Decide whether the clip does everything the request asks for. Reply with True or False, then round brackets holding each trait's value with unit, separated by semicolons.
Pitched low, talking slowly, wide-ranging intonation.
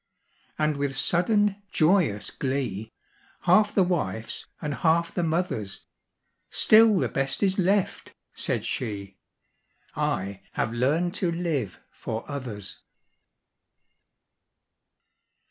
False (155 Hz; 100 wpm; 7.7 semitones)